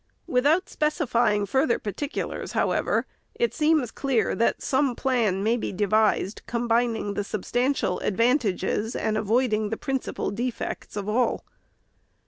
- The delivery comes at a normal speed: No, slow, 120 wpm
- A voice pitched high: Yes, high, 235 Hz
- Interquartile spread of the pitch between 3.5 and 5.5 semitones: Yes, average, 3.9 semitones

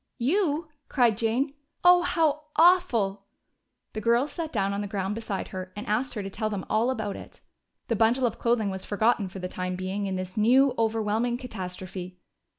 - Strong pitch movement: No, average, 4.6 semitones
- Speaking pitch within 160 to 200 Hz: No, high, 220 Hz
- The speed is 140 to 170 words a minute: No, average, 185 wpm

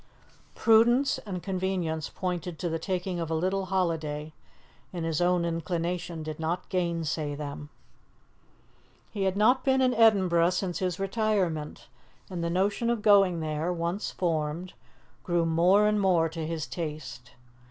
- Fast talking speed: No, average, 145 wpm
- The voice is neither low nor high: Yes, medium, 175 Hz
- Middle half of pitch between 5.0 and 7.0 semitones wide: No, average, 3.0 semitones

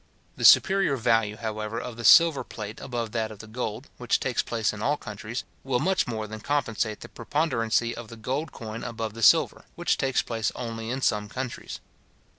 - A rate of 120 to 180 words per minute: No, average, 195 wpm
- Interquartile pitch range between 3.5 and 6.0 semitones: No, average, 2.8 semitones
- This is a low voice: Yes, low, 115 Hz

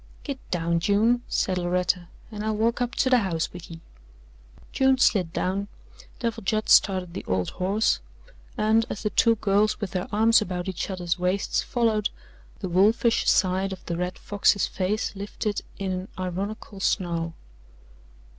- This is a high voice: Yes, high, 195 Hz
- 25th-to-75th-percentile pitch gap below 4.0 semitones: Yes, average, 3.1 semitones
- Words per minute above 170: No, average, 160 wpm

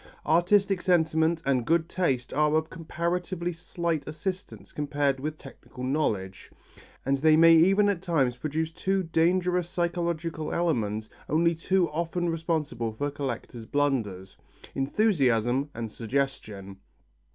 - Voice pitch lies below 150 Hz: No, medium, 155 Hz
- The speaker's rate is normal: No, slow, 120 wpm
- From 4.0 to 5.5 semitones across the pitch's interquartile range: Yes, average, 4.5 semitones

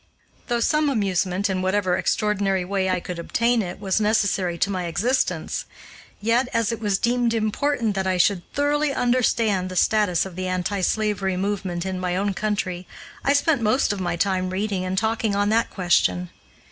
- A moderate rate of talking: Yes, average, 180 wpm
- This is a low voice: No, high, 200 Hz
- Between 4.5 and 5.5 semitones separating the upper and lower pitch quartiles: No, average, 3.5 semitones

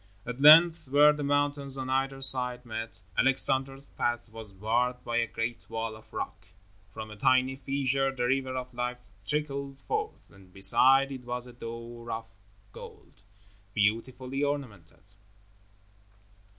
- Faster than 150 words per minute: No, average, 140 wpm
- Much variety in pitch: No, average, 2.9 semitones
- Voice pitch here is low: Yes, low, 130 Hz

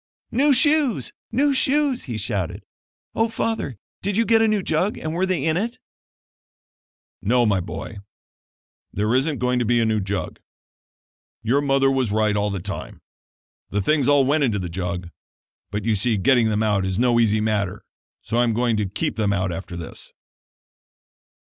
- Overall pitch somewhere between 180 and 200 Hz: No, low, 120 Hz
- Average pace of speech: Yes, average, 180 wpm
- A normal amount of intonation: No, wide, 7.5 semitones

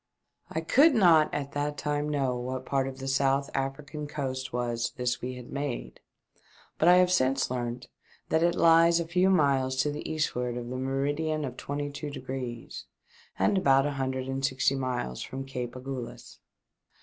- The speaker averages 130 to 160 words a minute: No, average, 175 wpm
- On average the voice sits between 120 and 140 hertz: Yes, low, 135 Hz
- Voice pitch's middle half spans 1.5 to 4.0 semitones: Yes, narrow, 2.6 semitones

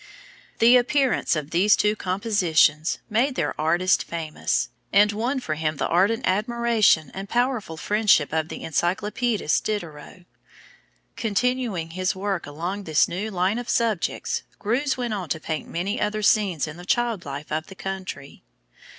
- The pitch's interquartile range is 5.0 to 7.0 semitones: Yes, wide, 5.5 semitones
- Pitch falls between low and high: No, high, 195 Hz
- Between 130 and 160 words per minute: Yes, average, 150 wpm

